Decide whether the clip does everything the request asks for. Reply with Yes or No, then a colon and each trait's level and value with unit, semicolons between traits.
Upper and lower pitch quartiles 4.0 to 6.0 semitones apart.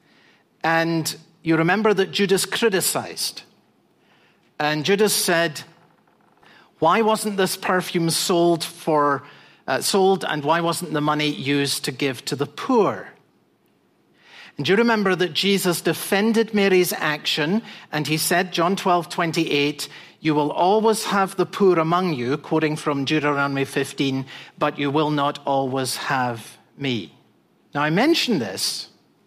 Yes: average, 4.4 semitones